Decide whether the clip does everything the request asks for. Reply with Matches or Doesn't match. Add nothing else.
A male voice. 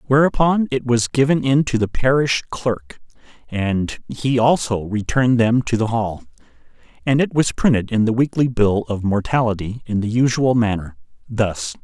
Matches